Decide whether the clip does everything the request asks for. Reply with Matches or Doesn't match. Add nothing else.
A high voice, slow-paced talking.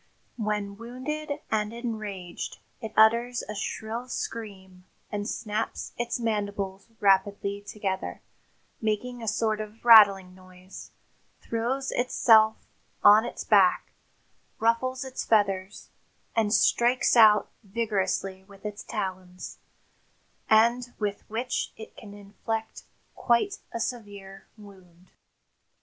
Matches